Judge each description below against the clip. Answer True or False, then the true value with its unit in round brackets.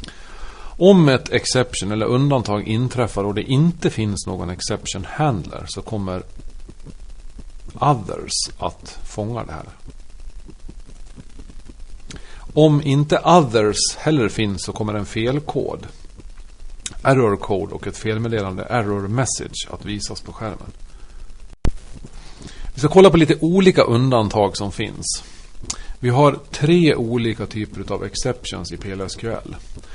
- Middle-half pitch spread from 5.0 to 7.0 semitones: True (5.4 semitones)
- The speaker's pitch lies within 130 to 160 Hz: False (110 Hz)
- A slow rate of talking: True (115 wpm)